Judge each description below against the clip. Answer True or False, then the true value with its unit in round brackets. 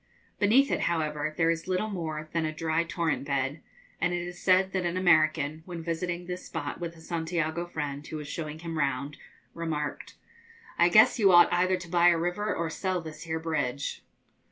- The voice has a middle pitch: True (165 Hz)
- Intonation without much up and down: True (2.3 semitones)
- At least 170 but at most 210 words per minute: True (195 wpm)